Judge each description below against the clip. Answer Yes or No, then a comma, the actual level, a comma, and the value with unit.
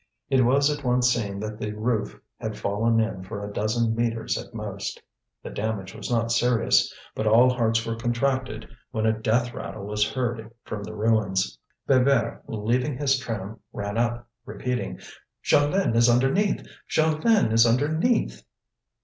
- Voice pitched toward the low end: Yes, low, 115 Hz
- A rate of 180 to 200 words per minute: No, average, 155 wpm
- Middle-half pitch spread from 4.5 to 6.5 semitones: No, average, 2.8 semitones